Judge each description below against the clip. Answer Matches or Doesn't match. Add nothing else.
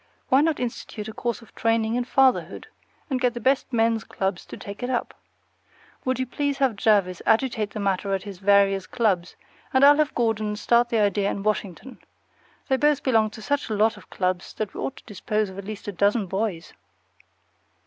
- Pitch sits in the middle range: Doesn't match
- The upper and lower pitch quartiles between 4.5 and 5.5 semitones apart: Doesn't match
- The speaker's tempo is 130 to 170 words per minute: Doesn't match